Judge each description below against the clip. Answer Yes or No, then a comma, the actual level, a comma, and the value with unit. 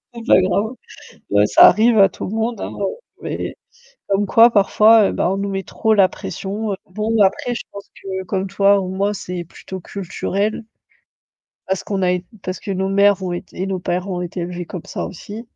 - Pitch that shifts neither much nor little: No, narrow, 2.1 semitones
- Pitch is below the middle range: No, high, 195 Hz